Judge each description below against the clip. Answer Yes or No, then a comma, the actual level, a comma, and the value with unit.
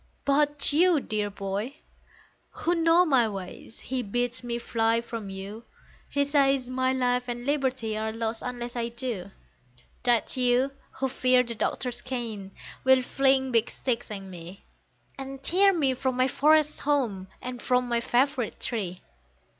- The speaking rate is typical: Yes, average, 155 wpm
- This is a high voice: Yes, very high, 250 Hz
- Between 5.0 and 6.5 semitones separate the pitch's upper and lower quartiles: No, average, 3.0 semitones